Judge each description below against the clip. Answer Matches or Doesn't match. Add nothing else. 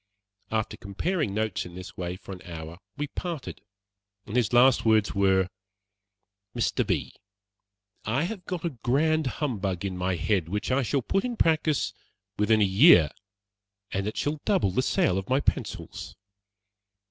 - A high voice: Doesn't match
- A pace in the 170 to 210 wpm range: Doesn't match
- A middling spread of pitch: Doesn't match